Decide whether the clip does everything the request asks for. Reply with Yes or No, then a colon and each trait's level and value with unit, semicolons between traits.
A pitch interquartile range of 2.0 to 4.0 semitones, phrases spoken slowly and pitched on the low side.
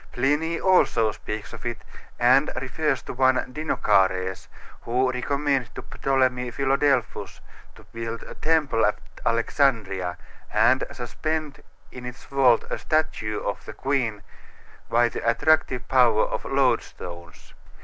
Yes: average, 3.4 semitones; slow, 125 wpm; low, 125 Hz